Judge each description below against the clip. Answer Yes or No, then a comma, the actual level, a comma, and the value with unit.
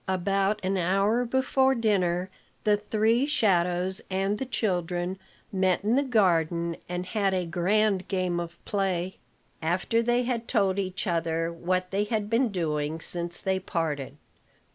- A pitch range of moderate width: Yes, average, 3.4 semitones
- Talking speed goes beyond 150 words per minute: No, average, 145 wpm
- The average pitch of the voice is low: No, high, 190 Hz